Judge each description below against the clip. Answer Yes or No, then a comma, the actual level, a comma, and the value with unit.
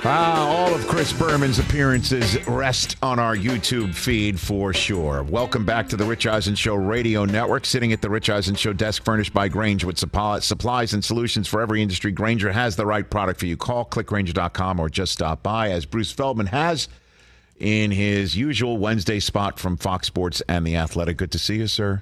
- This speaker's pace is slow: No, average, 195 wpm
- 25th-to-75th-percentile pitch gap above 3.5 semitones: No, average, 3.2 semitones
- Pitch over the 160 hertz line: No, low, 105 Hz